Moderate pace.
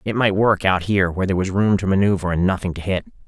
No: fast, 275 wpm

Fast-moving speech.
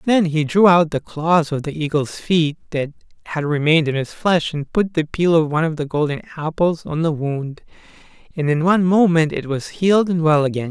Yes: fast, 220 wpm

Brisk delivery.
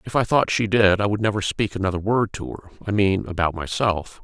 Yes: fast, 225 wpm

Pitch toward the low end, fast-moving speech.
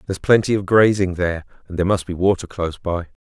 Yes: very low, 95 Hz; fast, 225 wpm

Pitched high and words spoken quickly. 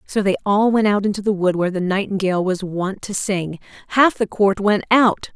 Yes: high, 200 Hz; fast, 225 wpm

